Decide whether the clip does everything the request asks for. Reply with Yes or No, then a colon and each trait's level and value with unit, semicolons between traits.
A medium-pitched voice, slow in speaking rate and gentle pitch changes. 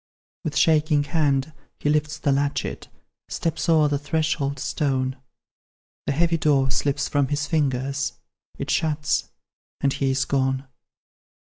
Yes: medium, 145 Hz; slow, 130 wpm; narrow, 2.1 semitones